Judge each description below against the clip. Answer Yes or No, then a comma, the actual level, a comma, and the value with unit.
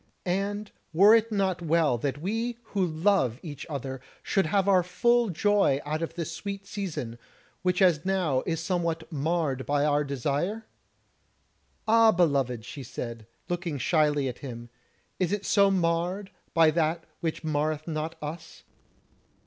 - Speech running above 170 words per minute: No, average, 150 wpm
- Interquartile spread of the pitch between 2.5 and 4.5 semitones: No, average, 4.9 semitones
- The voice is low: No, medium, 165 Hz